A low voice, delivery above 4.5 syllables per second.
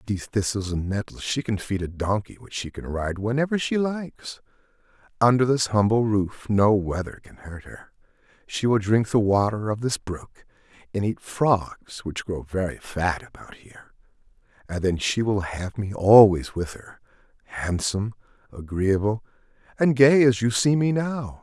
Yes: low, 110 Hz; 4.8 syllables/s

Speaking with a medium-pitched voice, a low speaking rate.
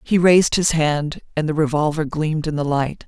No: medium, 155 Hz; fast, 215 wpm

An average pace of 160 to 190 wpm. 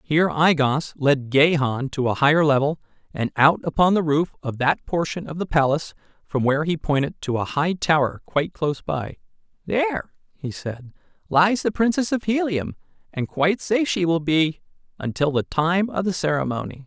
Yes: average, 180 wpm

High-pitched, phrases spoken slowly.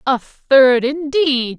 Yes: very high, 270 Hz; slow, 115 wpm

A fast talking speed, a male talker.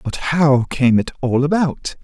No: average, 175 wpm; male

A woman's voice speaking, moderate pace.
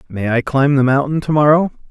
No: male; average, 190 wpm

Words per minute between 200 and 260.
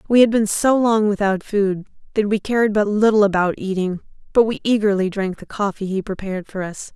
Yes: fast, 205 wpm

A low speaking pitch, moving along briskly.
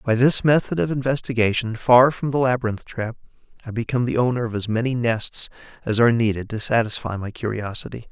No: low, 120 Hz; average, 185 wpm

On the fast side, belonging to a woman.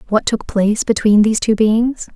No: average, 195 wpm; female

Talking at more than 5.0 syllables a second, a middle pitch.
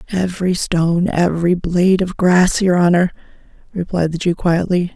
Yes: 5.2 syllables/s; medium, 180 Hz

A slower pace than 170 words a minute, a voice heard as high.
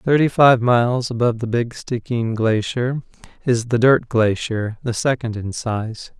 No: average, 155 wpm; low, 120 Hz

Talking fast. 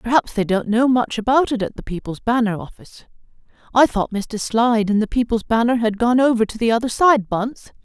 Yes: fast, 215 wpm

